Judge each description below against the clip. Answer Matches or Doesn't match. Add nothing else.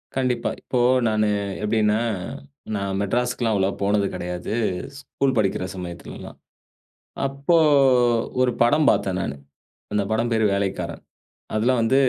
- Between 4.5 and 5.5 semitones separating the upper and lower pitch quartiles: Doesn't match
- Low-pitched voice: Matches